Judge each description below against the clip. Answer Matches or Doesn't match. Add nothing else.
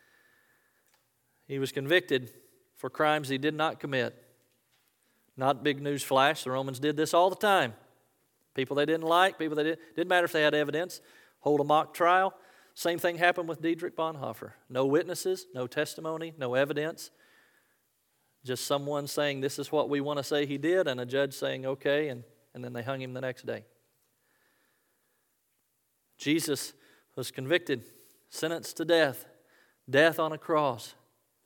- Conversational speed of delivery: Matches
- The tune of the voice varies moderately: Matches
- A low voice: Doesn't match